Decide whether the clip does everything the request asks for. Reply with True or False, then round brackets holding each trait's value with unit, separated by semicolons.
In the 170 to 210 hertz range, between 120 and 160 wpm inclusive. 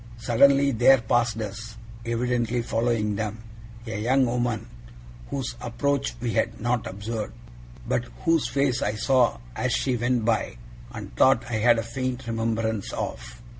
False (120 Hz; 145 wpm)